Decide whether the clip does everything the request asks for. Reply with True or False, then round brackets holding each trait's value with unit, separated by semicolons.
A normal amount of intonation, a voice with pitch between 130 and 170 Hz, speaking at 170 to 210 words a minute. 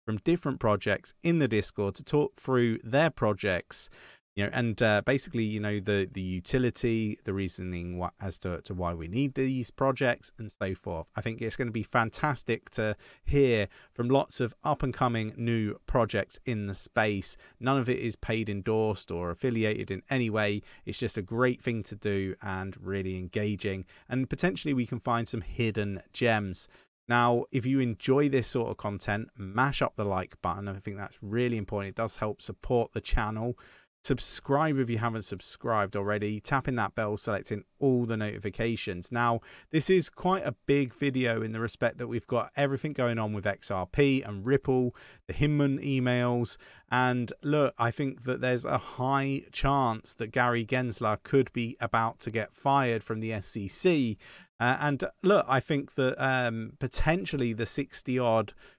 False (3.9 semitones; 115 Hz; 180 wpm)